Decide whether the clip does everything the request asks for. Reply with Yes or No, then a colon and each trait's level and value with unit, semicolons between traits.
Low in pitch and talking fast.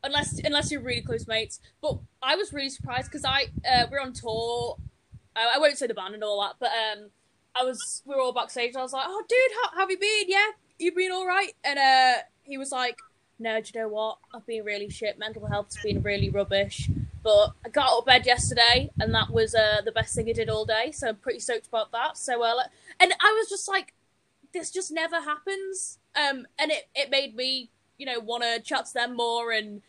No: very high, 255 Hz; fast, 240 wpm